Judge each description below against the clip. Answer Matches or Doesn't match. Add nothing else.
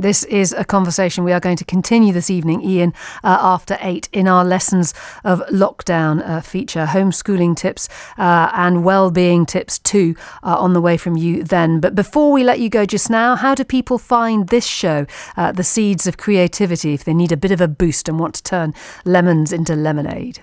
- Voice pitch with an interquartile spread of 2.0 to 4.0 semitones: Matches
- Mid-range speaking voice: Matches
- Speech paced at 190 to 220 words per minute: Matches